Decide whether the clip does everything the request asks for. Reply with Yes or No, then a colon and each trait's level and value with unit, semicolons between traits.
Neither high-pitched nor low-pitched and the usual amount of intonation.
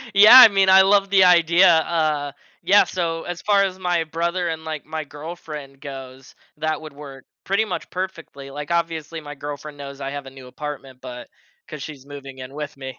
Yes: medium, 155 Hz; average, 3.9 semitones